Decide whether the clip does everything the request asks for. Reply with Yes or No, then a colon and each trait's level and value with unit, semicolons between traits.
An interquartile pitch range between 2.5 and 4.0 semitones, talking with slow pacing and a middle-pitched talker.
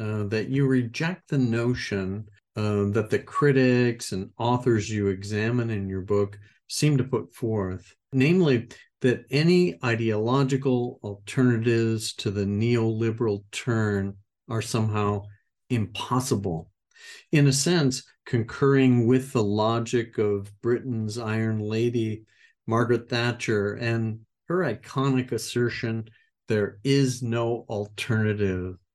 No: average, 3.1 semitones; slow, 110 wpm; low, 115 Hz